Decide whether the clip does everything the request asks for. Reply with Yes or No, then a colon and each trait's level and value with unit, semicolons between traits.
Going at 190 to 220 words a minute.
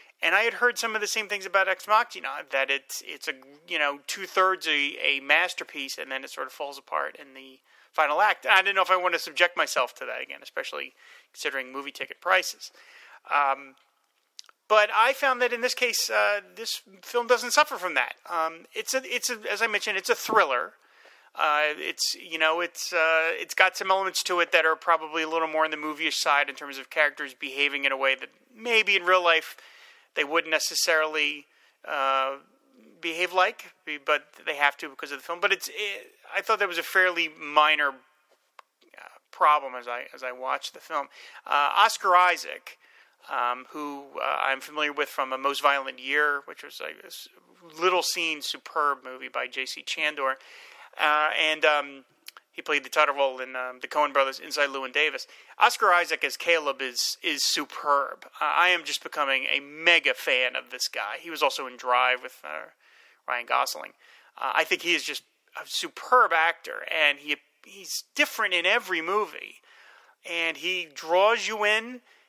Yes: average, 195 wpm